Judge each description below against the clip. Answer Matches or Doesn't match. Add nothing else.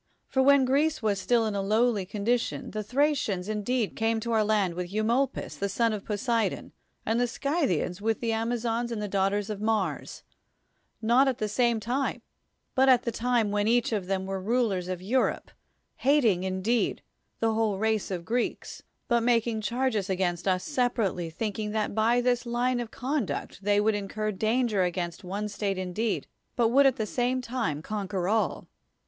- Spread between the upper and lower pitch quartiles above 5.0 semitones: Doesn't match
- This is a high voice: Matches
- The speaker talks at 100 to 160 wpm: Doesn't match